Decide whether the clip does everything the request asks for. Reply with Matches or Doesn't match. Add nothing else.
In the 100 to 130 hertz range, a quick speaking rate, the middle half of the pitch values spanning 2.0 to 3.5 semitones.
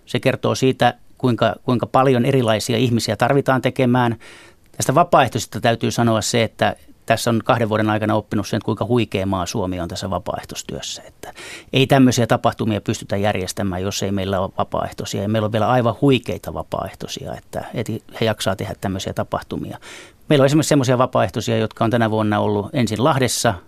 Matches